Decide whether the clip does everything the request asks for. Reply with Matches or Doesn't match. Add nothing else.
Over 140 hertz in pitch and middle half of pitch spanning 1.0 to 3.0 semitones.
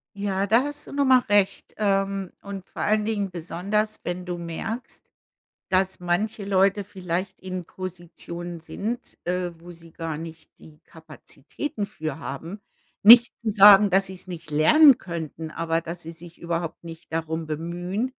Doesn't match